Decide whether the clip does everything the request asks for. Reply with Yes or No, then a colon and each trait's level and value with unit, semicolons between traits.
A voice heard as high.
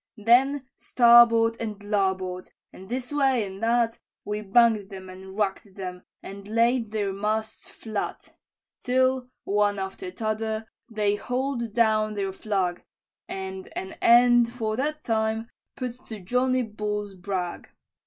Yes: high, 220 Hz